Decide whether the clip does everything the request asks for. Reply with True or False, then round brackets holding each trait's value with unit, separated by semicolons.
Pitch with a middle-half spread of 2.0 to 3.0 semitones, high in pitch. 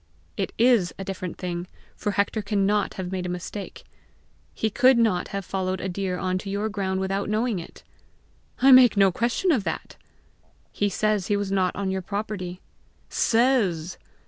True (2.5 semitones; 195 Hz)